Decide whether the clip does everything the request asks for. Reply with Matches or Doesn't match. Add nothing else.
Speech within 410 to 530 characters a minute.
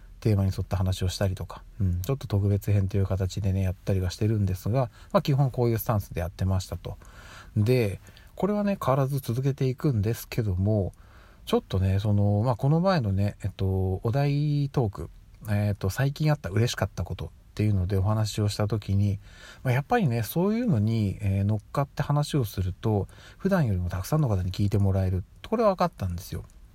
Matches